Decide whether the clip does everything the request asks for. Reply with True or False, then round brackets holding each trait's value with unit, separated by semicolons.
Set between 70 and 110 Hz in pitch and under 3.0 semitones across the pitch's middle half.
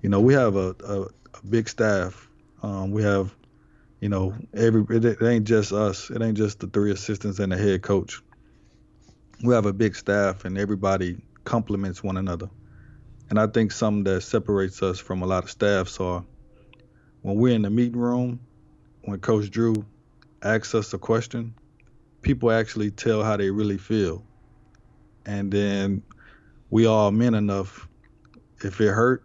True (105 Hz; 2.6 semitones)